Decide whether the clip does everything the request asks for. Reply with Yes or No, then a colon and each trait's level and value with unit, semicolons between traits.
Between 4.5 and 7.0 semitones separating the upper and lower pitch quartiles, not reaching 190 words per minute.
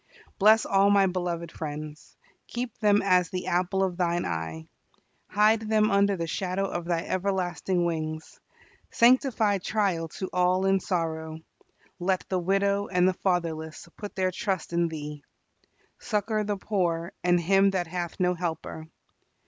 No: average, 2.8 semitones; average, 150 wpm